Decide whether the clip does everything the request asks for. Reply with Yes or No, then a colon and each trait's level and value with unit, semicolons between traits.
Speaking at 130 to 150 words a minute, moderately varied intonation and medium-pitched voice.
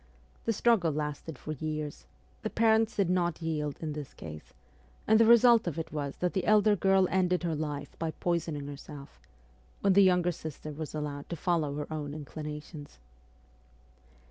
No: average, 170 wpm; average, 3.8 semitones; medium, 160 Hz